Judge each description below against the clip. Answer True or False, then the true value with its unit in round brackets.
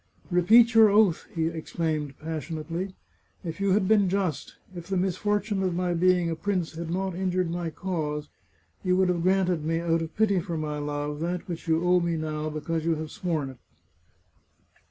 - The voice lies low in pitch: False (170 Hz)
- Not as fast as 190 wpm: False (195 wpm)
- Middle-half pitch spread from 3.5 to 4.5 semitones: False (2.8 semitones)